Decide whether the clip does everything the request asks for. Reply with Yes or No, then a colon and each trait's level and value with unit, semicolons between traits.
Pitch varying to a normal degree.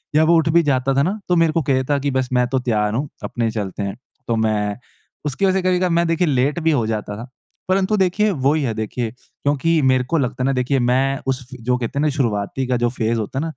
Yes: average, 4.7 semitones